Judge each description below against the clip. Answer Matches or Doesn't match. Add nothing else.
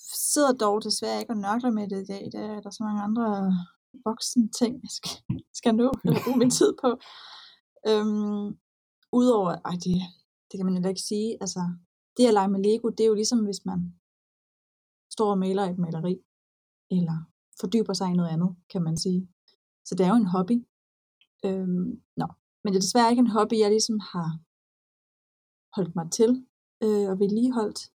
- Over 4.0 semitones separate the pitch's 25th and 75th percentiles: Doesn't match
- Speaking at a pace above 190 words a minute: Doesn't match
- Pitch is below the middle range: Doesn't match